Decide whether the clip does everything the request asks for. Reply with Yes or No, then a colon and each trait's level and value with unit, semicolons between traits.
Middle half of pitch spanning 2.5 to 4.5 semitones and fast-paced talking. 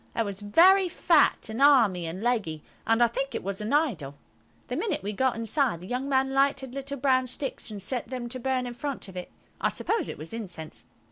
No: average, 5.1 semitones; fast, 220 wpm